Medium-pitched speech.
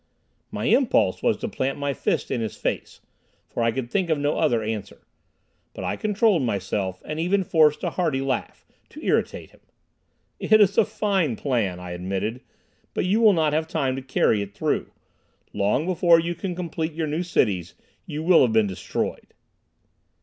Yes: medium, 150 Hz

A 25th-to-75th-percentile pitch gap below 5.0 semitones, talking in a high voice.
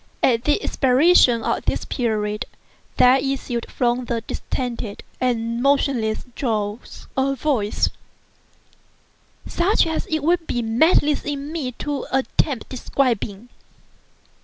Yes: average, 3.7 semitones; very high, 255 Hz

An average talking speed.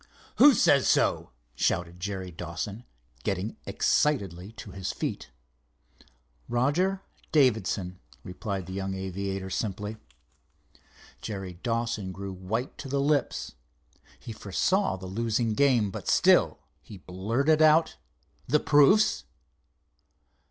No: slow, 110 wpm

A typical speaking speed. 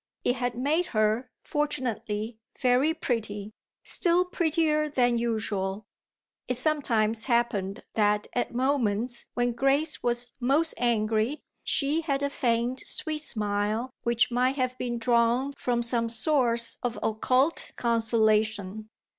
No: slow, 120 wpm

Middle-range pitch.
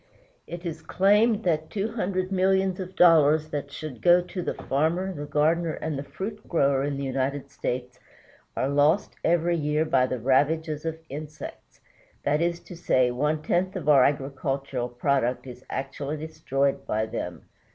Yes: medium, 155 Hz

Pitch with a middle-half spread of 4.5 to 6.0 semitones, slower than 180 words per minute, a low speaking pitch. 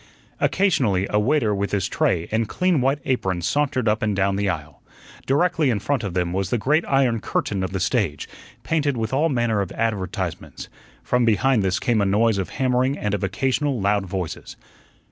No: wide, 5.4 semitones; average, 190 wpm; low, 110 Hz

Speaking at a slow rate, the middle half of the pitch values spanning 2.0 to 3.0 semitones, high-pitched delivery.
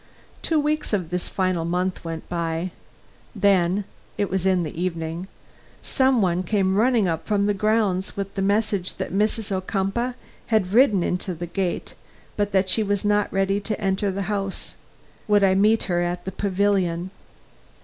No: average, 170 wpm; narrow, 2.4 semitones; high, 195 Hz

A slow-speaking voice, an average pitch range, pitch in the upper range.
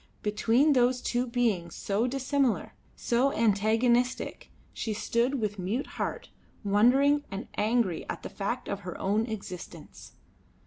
Yes: slow, 130 wpm; average, 3.5 semitones; high, 230 Hz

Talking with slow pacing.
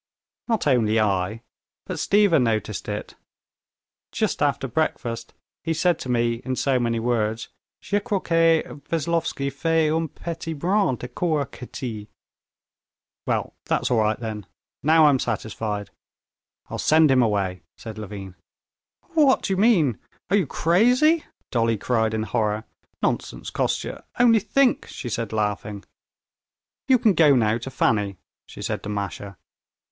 No: average, 145 wpm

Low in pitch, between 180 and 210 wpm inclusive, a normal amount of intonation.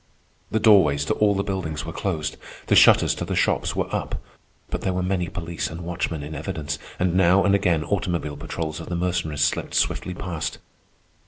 Yes: very low, 85 Hz; average, 190 wpm; average, 3.1 semitones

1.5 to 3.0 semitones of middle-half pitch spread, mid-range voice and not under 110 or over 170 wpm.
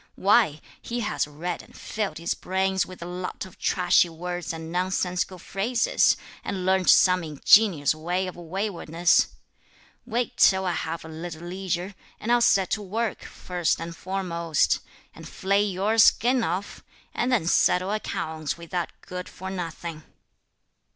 Yes: narrow, 2.6 semitones; medium, 180 Hz; average, 150 wpm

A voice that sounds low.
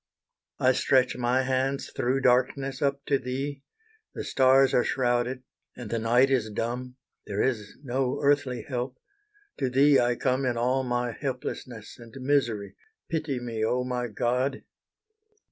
Yes: low, 125 Hz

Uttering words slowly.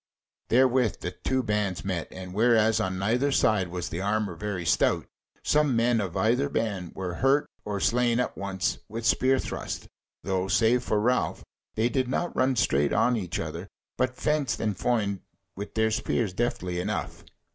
No: average, 170 wpm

